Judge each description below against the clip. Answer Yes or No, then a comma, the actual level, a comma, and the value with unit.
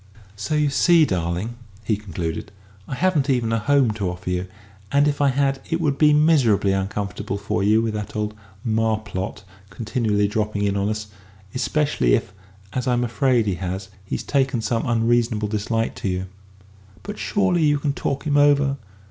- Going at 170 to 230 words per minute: Yes, average, 175 wpm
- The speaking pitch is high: No, low, 115 Hz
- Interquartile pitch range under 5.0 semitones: No, wide, 5.5 semitones